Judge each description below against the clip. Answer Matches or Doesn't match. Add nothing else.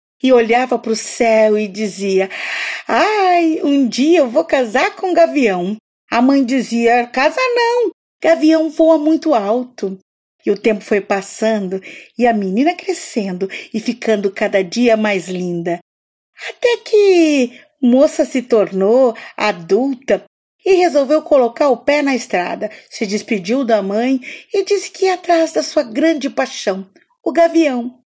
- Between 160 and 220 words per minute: Doesn't match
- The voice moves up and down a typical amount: Doesn't match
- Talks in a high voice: Matches